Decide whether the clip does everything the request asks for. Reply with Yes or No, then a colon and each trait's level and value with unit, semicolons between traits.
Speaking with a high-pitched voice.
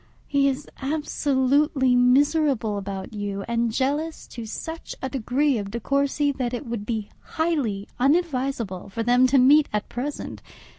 Yes: very high, 260 Hz